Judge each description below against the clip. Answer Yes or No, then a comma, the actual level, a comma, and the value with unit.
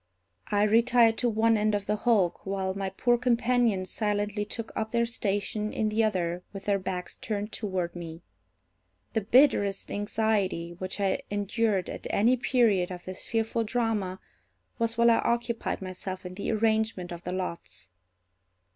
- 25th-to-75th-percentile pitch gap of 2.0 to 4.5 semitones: Yes, average, 3.3 semitones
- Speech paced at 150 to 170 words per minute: Yes, average, 160 wpm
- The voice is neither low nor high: No, high, 210 Hz